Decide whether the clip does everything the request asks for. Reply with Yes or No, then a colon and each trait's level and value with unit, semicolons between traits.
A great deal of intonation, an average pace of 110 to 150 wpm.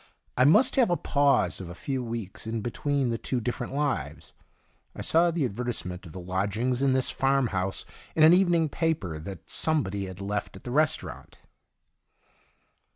No: wide, 6.9 semitones; average, 175 wpm